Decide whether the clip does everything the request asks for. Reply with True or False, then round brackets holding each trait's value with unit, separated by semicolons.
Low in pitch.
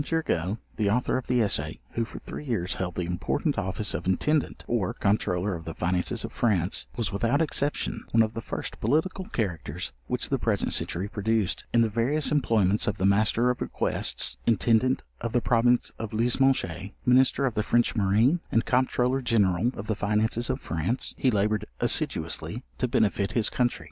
True (110 Hz)